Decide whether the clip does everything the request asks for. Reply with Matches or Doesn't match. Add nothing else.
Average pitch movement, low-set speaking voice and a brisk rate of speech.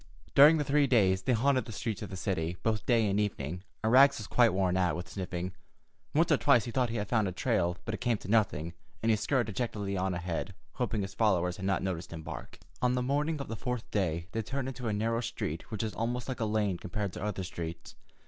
Matches